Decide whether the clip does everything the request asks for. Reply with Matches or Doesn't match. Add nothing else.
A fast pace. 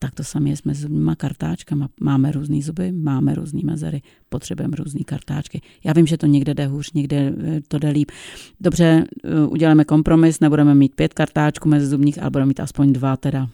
Matches